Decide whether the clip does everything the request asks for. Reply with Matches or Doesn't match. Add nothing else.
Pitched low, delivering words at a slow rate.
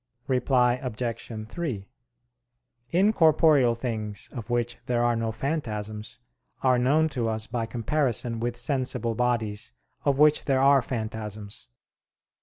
Matches